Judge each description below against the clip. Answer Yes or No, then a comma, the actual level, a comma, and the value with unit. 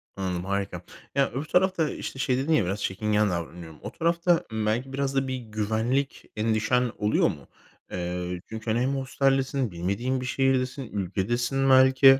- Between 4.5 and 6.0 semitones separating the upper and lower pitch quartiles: Yes, average, 4.8 semitones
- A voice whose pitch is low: Yes, low, 125 Hz